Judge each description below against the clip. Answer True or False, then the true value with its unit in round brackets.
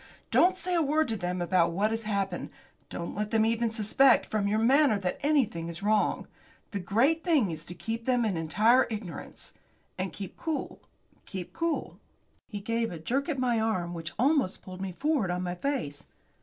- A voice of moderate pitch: False (215 Hz)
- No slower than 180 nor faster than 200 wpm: True (190 wpm)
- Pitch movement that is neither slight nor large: False (6.3 semitones)